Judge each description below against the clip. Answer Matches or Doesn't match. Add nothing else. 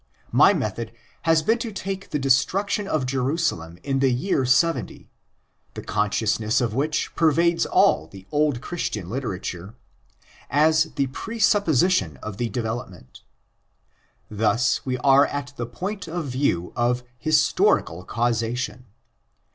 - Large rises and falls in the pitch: Matches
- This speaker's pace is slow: Matches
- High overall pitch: Doesn't match